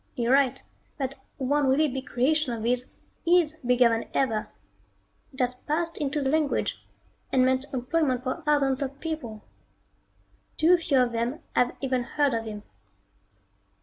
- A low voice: No, very high, 265 Hz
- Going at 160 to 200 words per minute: No, average, 150 wpm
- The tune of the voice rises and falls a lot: No, average, 3.1 semitones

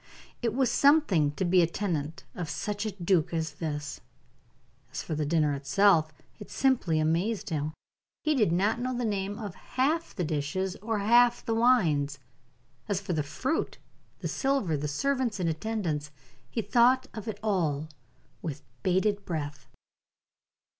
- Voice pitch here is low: No, high, 190 Hz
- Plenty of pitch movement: Yes, wide, 6.4 semitones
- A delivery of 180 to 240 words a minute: No, average, 155 wpm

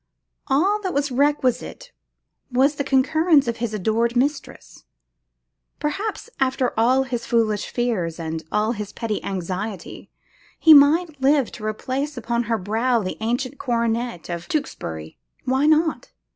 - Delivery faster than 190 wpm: No, slow, 135 wpm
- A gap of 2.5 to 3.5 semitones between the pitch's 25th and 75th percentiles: No, average, 4.6 semitones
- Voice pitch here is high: Yes, high, 245 Hz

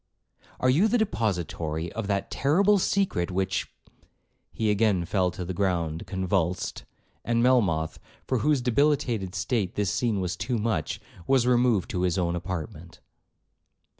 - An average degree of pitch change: No, wide, 5.7 semitones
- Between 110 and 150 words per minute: Yes, average, 140 wpm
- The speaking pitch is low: Yes, low, 100 Hz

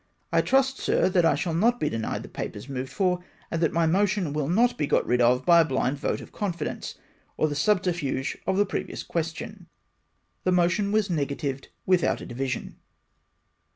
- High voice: No, medium, 170 Hz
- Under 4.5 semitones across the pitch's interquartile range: No, average, 5.2 semitones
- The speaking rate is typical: Yes, average, 190 wpm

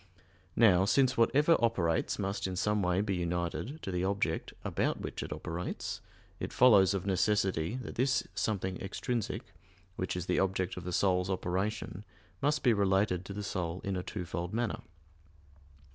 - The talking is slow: No, average, 160 wpm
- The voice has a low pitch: Yes, very low, 95 Hz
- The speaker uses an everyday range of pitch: Yes, average, 3.1 semitones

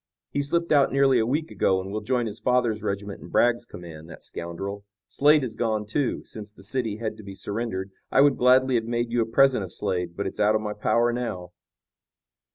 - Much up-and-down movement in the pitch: No, average, 3.9 semitones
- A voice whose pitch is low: Yes, low, 110 Hz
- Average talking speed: No, fast, 220 wpm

